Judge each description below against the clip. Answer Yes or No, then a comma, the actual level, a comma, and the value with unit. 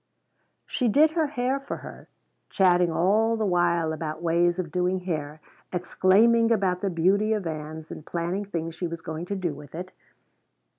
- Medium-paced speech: Yes, average, 170 wpm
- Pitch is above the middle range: No, medium, 180 Hz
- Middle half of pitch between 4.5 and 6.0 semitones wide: No, average, 3.7 semitones